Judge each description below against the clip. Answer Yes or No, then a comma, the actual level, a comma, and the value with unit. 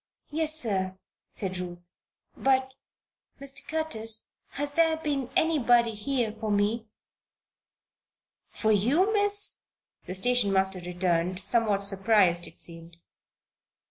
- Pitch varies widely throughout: Yes, wide, 6.5 semitones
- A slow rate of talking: Yes, slow, 110 wpm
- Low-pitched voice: No, high, 220 Hz